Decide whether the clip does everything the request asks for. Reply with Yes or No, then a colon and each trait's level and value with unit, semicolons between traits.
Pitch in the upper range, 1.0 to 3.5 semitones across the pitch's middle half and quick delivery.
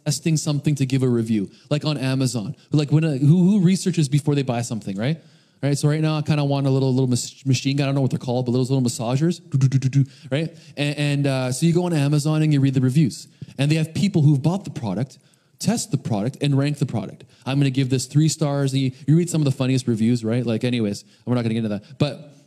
No: medium, 140 Hz; average, 2.7 semitones; fast, 265 wpm